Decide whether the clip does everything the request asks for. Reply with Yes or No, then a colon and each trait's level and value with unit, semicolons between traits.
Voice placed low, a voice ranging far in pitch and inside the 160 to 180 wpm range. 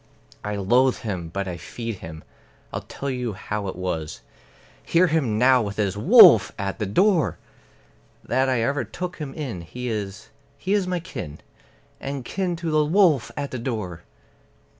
Yes: low, 120 Hz; wide, 7.5 semitones; average, 170 wpm